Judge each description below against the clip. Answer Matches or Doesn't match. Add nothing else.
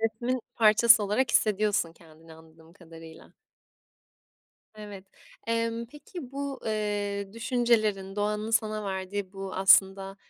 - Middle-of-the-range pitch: Doesn't match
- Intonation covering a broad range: Doesn't match